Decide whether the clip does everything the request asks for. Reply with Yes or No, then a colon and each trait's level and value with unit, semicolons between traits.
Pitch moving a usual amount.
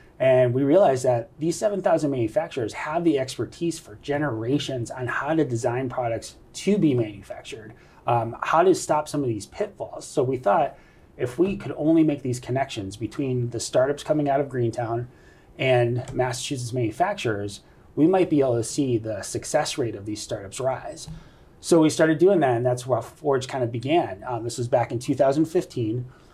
Yes: average, 4.1 semitones